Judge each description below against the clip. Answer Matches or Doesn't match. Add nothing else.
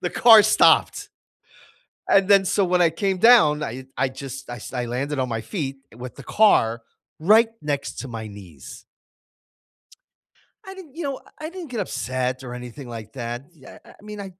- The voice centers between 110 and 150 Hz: Matches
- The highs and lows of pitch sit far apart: Matches